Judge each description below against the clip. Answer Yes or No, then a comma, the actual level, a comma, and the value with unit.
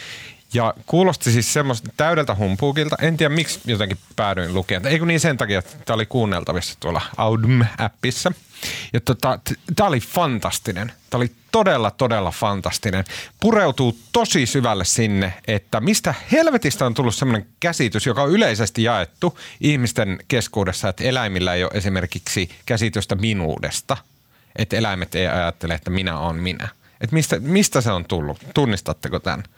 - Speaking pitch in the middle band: No, low, 115 Hz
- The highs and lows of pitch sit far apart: Yes, wide, 6.2 semitones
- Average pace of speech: Yes, average, 145 wpm